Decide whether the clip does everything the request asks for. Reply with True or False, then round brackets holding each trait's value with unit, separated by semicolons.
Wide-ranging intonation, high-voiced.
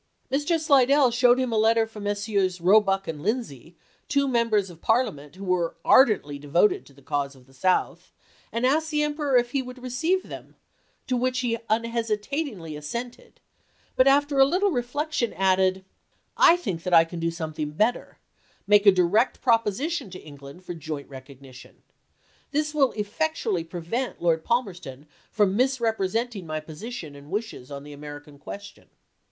True (7.4 semitones; 210 Hz)